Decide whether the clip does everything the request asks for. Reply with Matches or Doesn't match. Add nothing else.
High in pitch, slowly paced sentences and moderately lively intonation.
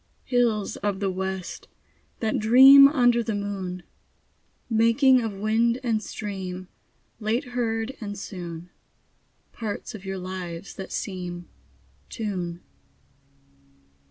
Matches